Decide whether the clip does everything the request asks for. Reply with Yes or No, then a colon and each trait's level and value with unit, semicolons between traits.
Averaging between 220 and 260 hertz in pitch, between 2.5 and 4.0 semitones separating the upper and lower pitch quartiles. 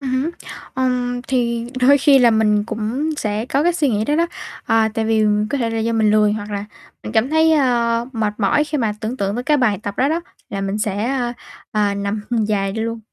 Yes: high, 230 Hz; average, 3.5 semitones